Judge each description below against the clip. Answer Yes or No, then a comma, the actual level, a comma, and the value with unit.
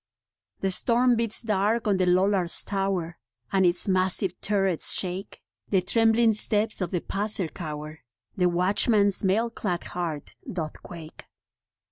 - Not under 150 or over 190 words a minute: No, slow, 135 wpm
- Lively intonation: No, average, 3.0 semitones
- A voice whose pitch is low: No, high, 190 Hz